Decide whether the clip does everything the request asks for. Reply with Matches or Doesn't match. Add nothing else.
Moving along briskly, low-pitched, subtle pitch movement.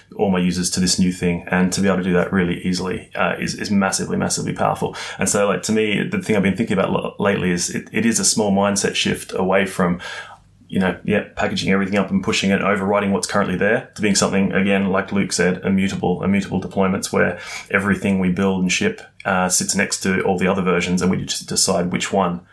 Matches